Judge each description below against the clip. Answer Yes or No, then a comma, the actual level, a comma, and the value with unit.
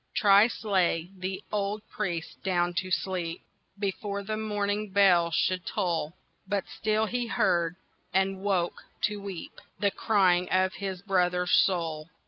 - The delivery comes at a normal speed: No, slow, 130 wpm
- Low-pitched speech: No, high, 190 Hz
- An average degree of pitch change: No, narrow, 2.3 semitones